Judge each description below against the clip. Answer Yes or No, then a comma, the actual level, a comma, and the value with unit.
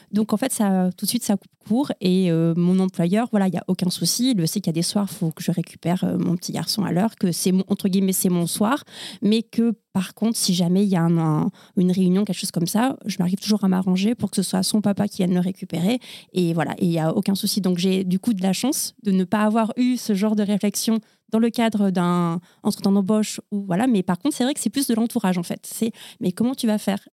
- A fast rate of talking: Yes, fast, 285 wpm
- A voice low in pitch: No, high, 200 Hz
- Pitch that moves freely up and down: No, average, 3.1 semitones